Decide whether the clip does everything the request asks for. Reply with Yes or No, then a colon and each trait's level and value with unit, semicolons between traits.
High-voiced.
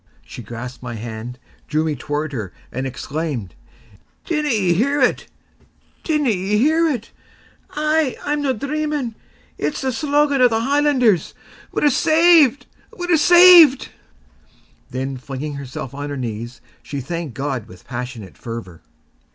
No: medium, 180 Hz